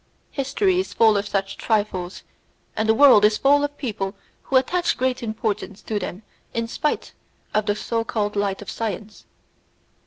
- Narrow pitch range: No, average, 4.1 semitones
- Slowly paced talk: No, average, 165 wpm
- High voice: Yes, high, 220 Hz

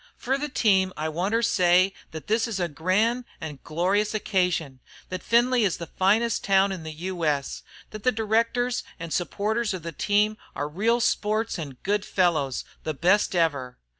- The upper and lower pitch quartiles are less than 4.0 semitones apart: No, average, 4.9 semitones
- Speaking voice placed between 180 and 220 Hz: Yes, high, 190 Hz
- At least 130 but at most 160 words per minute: No, average, 175 wpm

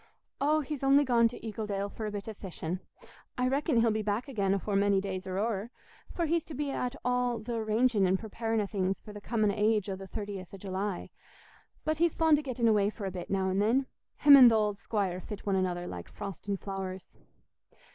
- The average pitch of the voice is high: Yes, high, 210 Hz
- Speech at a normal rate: No, fast, 225 wpm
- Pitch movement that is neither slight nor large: Yes, average, 4.0 semitones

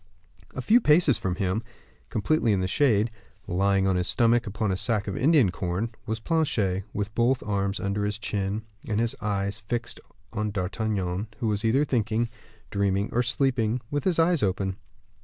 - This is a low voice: Yes, low, 105 Hz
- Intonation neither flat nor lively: Yes, average, 3.3 semitones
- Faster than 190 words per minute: No, average, 175 wpm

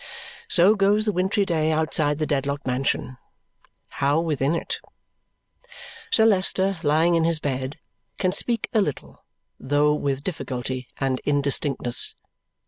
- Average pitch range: Yes, average, 4.9 semitones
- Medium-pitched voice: Yes, medium, 155 Hz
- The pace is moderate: No, slow, 130 wpm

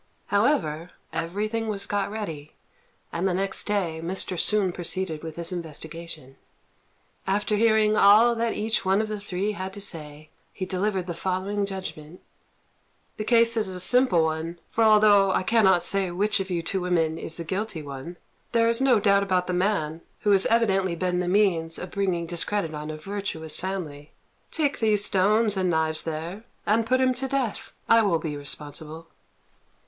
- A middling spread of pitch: Yes, average, 4.2 semitones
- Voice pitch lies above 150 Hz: Yes, high, 190 Hz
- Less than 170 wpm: No, average, 175 wpm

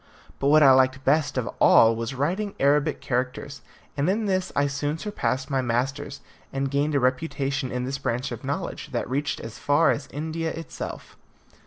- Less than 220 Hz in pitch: Yes, medium, 140 Hz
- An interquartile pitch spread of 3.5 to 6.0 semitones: No, average, 2.8 semitones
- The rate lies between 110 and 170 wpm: No, average, 180 wpm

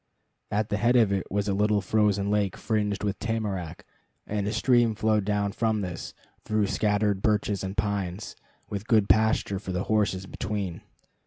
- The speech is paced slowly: No, average, 170 wpm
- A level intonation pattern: Yes, narrow, 1.6 semitones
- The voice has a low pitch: Yes, low, 105 Hz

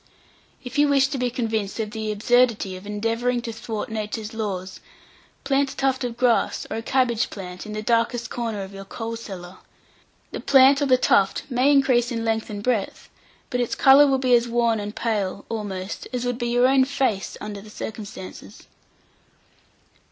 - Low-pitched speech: No, high, 230 Hz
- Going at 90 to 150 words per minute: No, average, 185 wpm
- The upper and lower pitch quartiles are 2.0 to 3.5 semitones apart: Yes, average, 3.1 semitones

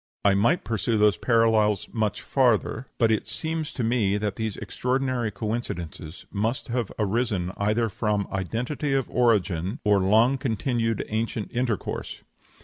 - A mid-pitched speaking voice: No, low, 110 Hz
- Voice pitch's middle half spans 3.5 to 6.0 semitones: No, average, 3.0 semitones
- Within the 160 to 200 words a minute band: No, average, 140 wpm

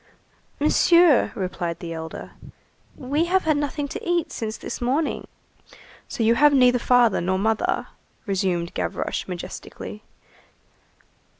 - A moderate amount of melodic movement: No, wide, 7.7 semitones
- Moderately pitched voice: No, high, 240 Hz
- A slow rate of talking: Yes, slow, 120 wpm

